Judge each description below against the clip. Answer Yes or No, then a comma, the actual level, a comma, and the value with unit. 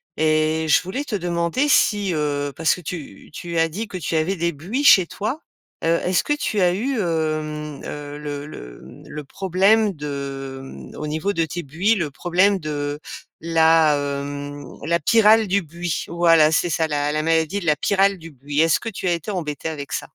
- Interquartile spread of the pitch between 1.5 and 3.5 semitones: No, average, 4.0 semitones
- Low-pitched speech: No, medium, 165 Hz